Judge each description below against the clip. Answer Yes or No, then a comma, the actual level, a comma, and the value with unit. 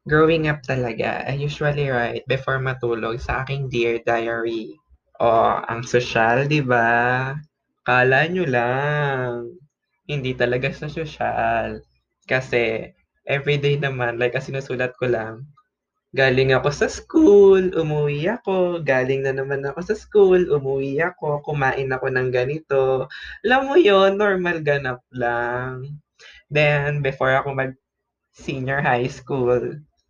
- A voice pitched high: No, low, 135 Hz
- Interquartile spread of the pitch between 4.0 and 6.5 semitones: No, average, 3.2 semitones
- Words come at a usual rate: Yes, average, 120 wpm